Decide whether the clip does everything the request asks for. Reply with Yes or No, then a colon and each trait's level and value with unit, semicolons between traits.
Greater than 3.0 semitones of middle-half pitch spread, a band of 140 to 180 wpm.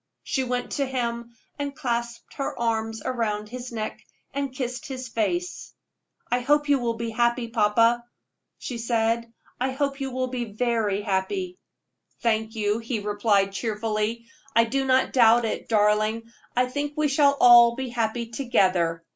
No: narrow, 2.6 semitones; average, 155 wpm